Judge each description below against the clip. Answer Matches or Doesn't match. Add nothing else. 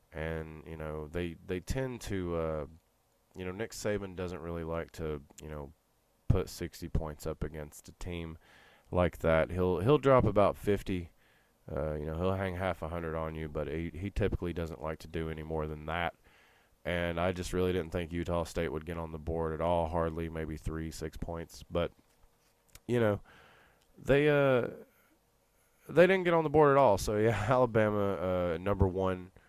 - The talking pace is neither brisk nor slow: Matches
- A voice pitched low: Matches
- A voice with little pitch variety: Doesn't match